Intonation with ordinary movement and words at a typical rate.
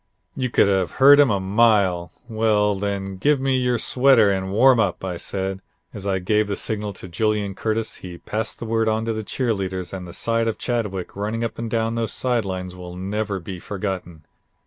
No: average, 3.1 semitones; fast, 215 wpm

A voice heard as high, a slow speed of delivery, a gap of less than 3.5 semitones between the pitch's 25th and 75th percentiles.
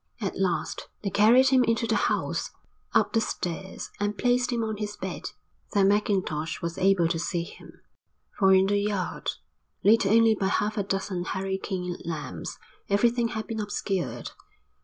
No: high, 200 Hz; average, 160 wpm; average, 2.7 semitones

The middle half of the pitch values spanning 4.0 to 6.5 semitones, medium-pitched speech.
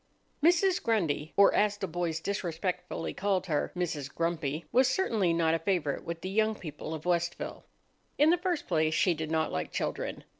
Yes: average, 4.3 semitones; medium, 175 Hz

